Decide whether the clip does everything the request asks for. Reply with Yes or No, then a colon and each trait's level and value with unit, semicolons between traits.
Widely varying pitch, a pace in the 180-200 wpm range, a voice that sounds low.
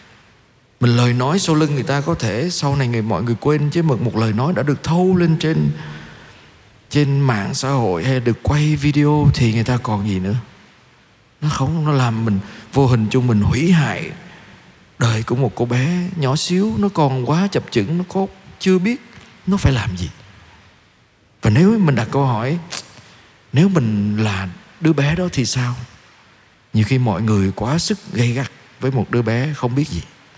Yes: wide, 5.7 semitones; average, 195 wpm; low, 130 Hz